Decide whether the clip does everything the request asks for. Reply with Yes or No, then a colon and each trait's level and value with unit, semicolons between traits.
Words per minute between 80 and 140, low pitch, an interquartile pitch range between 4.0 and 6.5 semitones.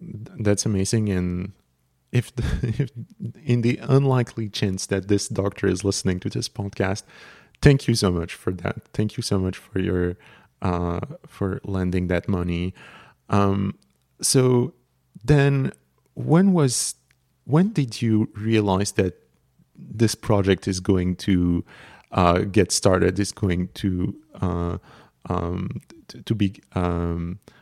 Yes: slow, 135 wpm; low, 100 Hz; average, 4.5 semitones